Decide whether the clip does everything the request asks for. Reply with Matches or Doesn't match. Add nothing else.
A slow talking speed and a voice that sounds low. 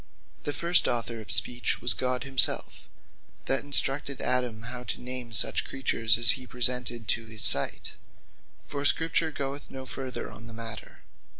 Doesn't match